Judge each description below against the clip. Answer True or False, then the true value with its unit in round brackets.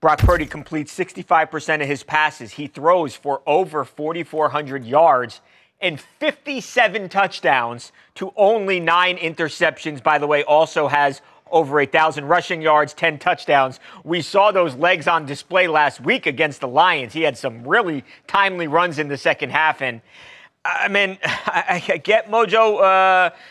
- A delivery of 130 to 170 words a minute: True (155 wpm)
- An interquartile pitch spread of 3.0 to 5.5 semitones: True (3.8 semitones)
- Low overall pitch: False (160 Hz)